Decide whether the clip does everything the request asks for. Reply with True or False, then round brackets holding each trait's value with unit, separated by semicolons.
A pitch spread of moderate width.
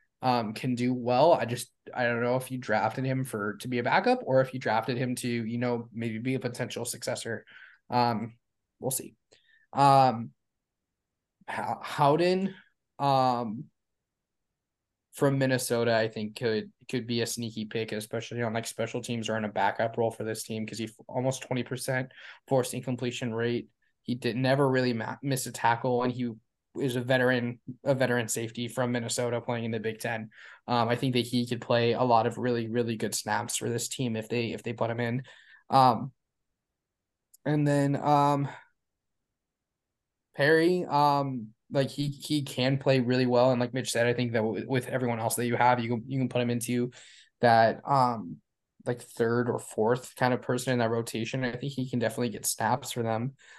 False (2.0 semitones)